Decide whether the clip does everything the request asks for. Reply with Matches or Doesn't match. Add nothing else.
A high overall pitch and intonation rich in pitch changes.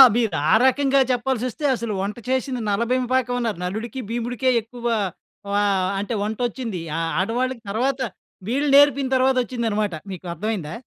Doesn't match